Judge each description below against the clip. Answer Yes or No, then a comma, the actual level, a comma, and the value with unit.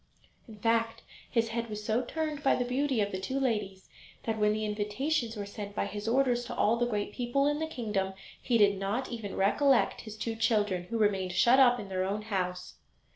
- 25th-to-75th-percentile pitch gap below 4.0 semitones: Yes, average, 3.1 semitones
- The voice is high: Yes, high, 225 Hz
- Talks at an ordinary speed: No, fast, 215 wpm